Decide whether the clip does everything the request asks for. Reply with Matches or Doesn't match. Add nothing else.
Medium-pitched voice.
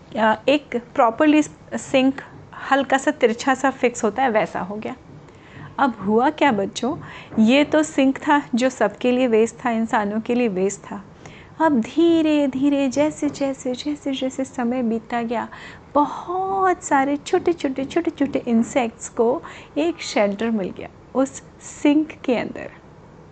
Doesn't match